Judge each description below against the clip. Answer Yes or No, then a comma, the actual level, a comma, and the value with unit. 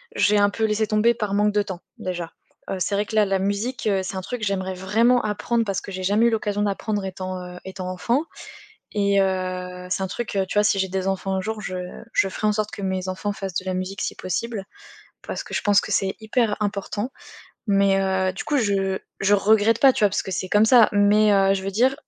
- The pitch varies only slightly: Yes, narrow, 2.0 semitones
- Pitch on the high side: Yes, high, 200 Hz